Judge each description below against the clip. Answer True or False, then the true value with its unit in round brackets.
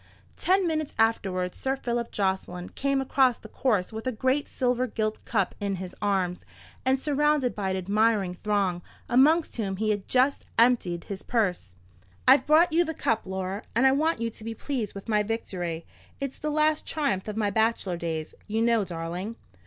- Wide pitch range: True (5.7 semitones)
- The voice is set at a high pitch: True (225 Hz)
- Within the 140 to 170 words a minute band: False (185 wpm)